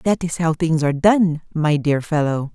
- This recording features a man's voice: No, female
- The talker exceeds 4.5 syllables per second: Yes, 4.8 syllables/s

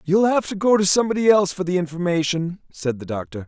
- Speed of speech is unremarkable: No, fast, 225 wpm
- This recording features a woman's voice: No, male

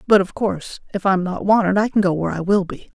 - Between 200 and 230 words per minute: No, fast, 280 wpm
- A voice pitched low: No, high, 195 Hz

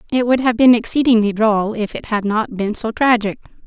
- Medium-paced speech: No, fast, 215 wpm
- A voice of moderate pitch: No, high, 225 Hz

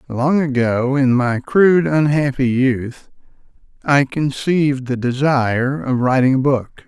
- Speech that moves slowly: Yes, slow, 130 wpm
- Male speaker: Yes, male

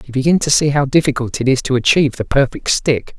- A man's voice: Yes, male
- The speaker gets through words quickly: Yes, fast, 245 wpm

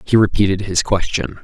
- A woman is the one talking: No, male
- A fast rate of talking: No, average, 165 wpm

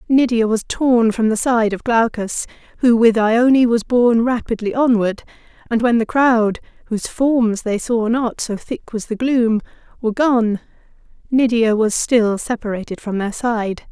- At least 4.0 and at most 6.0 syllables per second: No, 3.7 syllables/s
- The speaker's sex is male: No, female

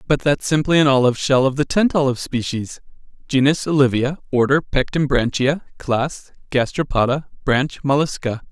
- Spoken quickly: No, slow, 135 wpm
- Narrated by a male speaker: Yes, male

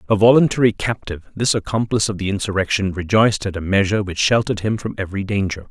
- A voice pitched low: Yes, low, 100 Hz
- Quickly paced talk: No, average, 190 wpm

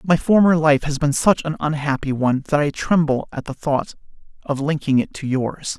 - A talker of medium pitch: Yes, medium, 150 Hz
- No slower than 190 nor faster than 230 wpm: Yes, fast, 205 wpm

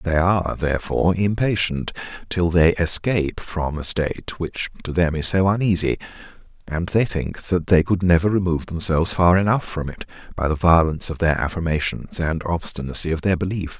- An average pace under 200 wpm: Yes, average, 175 wpm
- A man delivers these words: Yes, male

